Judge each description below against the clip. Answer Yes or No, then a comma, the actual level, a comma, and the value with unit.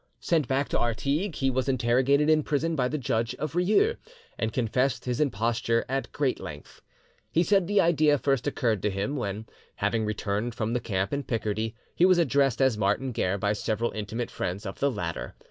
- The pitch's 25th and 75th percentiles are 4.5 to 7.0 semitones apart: Yes, average, 4.8 semitones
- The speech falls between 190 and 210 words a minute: Yes, average, 195 wpm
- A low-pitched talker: Yes, low, 125 Hz